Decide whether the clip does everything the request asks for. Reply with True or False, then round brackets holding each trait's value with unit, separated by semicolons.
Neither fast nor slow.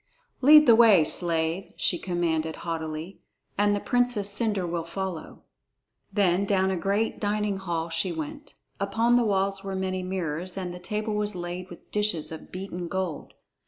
True (165 wpm)